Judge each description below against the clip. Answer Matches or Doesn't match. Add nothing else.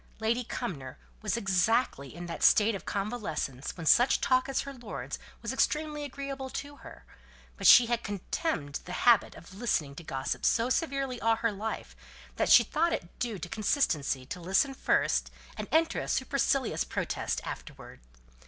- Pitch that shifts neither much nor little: Doesn't match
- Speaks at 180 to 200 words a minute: Doesn't match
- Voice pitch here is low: Doesn't match